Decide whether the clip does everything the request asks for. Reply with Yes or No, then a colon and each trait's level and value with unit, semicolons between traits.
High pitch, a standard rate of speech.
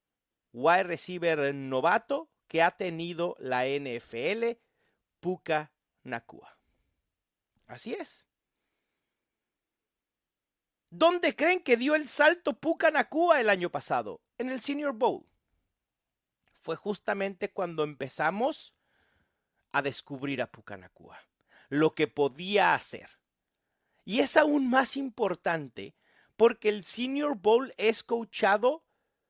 No: high, 205 Hz; slow, 105 wpm